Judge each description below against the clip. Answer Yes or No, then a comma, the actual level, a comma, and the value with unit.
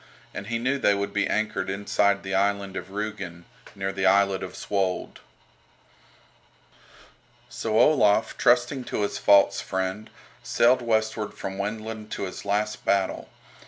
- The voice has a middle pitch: No, low, 100 Hz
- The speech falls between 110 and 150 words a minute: Yes, average, 140 wpm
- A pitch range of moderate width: No, narrow, 1.9 semitones